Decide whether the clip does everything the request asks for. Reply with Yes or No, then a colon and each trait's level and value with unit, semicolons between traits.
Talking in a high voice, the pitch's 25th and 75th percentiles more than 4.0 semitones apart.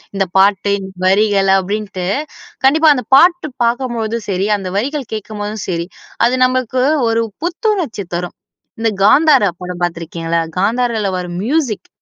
Yes: high, 215 Hz; average, 5.0 semitones